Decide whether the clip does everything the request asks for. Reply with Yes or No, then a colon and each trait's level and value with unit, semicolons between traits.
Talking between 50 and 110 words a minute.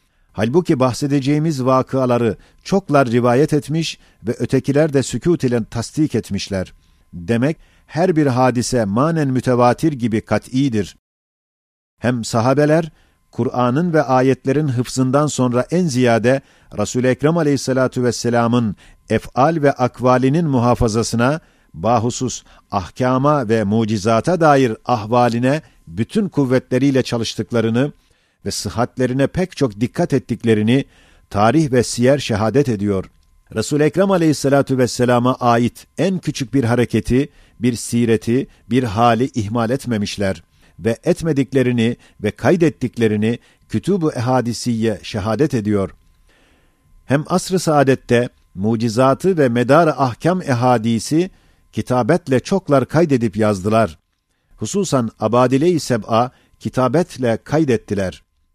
Yes: average, 100 wpm